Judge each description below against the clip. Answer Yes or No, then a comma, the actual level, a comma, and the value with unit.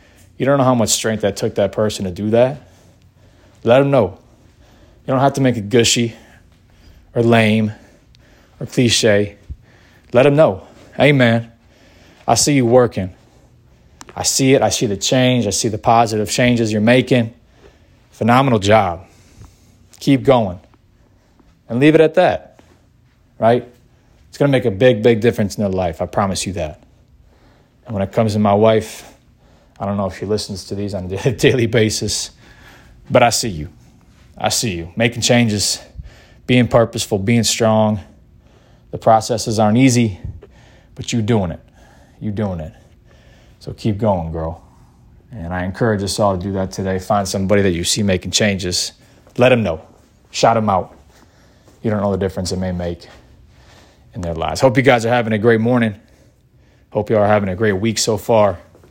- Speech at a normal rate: Yes, average, 175 wpm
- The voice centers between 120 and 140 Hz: No, low, 110 Hz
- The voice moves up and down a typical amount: Yes, average, 3.8 semitones